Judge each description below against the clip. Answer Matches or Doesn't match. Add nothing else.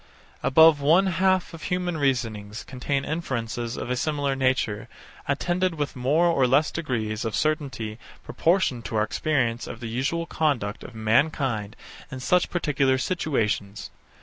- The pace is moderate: Matches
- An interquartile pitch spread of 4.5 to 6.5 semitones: Matches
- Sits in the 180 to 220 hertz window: Doesn't match